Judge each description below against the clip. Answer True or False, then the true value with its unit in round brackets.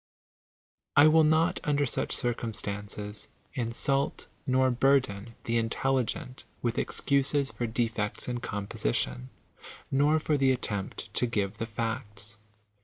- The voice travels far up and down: False (4.3 semitones)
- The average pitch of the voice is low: True (120 Hz)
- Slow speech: True (115 wpm)